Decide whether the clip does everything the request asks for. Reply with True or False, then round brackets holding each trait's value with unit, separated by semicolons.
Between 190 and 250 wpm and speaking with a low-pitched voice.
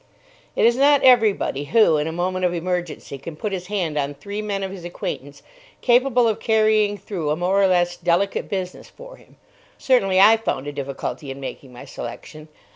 False (195 wpm; 185 Hz)